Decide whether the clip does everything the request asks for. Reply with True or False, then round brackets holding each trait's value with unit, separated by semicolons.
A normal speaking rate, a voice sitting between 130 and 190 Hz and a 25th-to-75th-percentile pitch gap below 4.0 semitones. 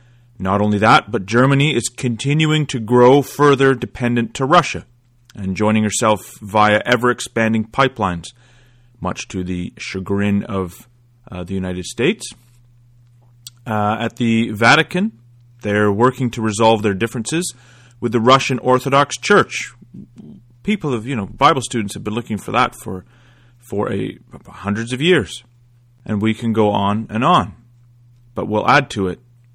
False (145 wpm; 120 Hz; 2.6 semitones)